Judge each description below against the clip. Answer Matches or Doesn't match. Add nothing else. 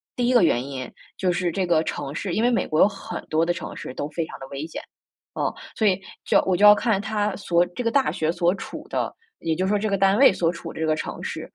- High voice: Doesn't match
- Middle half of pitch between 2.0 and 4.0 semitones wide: Doesn't match